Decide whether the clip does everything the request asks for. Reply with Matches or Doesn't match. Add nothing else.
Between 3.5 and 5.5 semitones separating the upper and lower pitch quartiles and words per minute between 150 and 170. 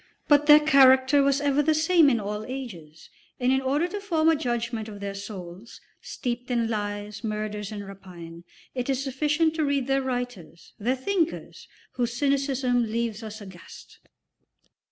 Matches